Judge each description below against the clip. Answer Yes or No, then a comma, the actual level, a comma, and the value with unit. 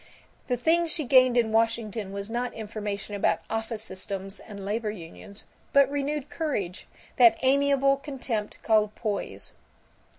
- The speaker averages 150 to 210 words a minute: No, slow, 135 wpm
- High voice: Yes, high, 225 Hz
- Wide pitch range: No, average, 4.8 semitones